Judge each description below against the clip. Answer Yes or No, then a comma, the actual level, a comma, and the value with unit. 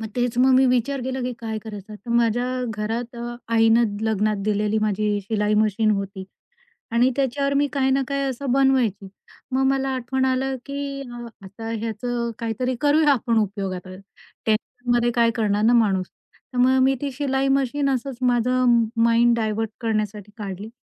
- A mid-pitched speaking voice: No, high, 235 Hz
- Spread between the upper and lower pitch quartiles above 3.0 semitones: Yes, average, 3.4 semitones